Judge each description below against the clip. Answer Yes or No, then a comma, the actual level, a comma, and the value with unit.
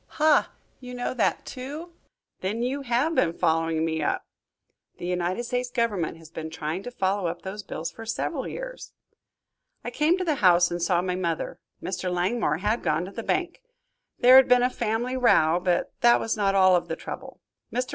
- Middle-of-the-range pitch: No, high, 205 Hz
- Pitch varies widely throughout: Yes, wide, 6.1 semitones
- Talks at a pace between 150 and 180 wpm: No, average, 195 wpm